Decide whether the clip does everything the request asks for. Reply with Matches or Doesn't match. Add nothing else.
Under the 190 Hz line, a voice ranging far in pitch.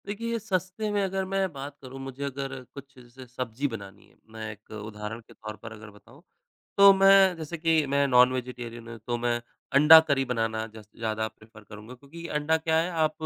Matches